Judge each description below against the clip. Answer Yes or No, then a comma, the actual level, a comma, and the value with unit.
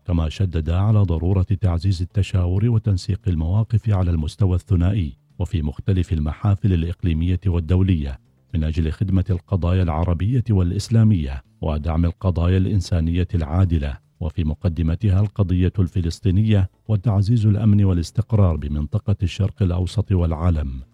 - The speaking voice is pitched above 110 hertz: No, very low, 90 Hz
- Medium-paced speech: Yes, average, 105 wpm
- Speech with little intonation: No, average, 3.2 semitones